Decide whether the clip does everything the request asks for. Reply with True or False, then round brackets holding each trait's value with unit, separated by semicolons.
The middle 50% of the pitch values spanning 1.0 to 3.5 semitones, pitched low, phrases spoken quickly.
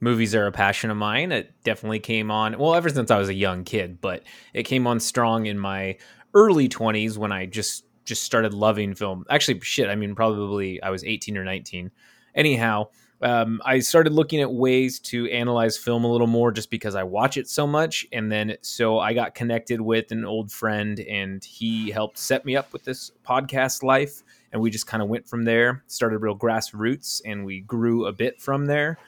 True (2.8 semitones; 115 Hz; 210 wpm)